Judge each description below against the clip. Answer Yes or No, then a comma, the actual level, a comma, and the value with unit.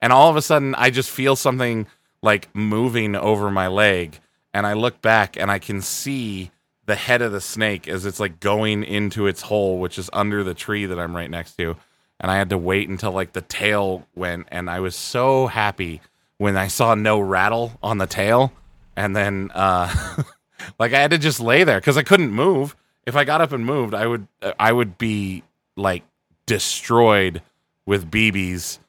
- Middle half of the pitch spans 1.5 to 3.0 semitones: No, average, 3.7 semitones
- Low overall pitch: Yes, low, 105 Hz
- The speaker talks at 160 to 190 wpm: No, average, 200 wpm